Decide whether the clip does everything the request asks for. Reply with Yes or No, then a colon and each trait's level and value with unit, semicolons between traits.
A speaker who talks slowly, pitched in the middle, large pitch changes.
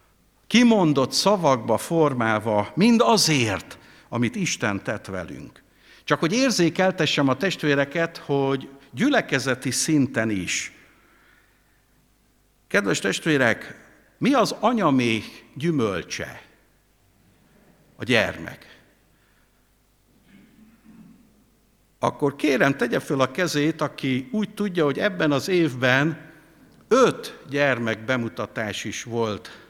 Yes: slow, 90 wpm; medium, 145 Hz; wide, 6.3 semitones